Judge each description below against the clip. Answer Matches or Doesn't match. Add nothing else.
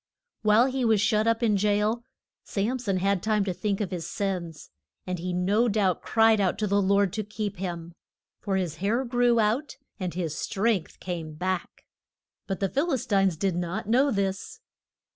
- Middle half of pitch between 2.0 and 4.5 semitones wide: Matches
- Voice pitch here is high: Matches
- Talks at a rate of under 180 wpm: Doesn't match